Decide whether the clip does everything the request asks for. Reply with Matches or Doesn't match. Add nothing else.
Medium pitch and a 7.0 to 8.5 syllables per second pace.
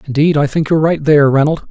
Matches